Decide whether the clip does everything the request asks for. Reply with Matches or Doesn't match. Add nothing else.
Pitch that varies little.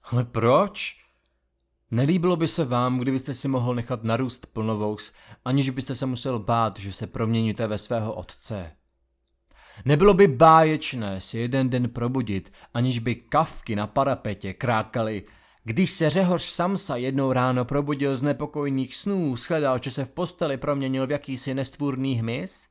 Doesn't match